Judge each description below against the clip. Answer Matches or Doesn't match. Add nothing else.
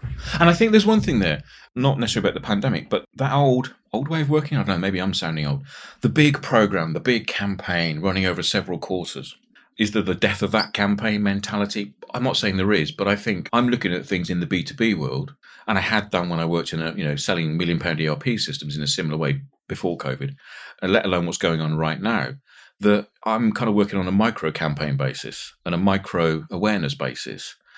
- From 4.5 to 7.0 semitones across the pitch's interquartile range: Matches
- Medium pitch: Doesn't match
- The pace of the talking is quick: Matches